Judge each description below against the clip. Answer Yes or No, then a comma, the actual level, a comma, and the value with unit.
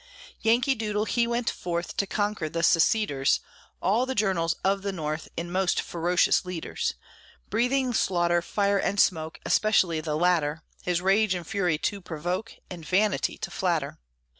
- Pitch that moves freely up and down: No, average, 4.0 semitones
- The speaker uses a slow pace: No, average, 155 wpm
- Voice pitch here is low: No, medium, 185 Hz